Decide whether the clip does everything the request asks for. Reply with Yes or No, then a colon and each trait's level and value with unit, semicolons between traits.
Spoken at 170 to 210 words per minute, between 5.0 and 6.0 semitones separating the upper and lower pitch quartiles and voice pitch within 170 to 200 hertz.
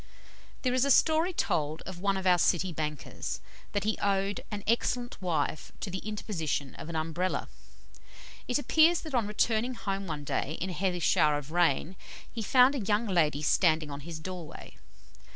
Yes: average, 180 wpm; wide, 5.6 semitones; high, 190 Hz